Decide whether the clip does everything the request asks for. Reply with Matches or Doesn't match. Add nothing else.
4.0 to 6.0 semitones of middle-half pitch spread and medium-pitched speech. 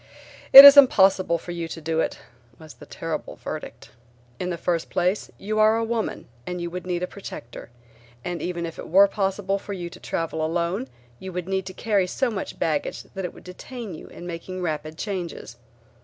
Doesn't match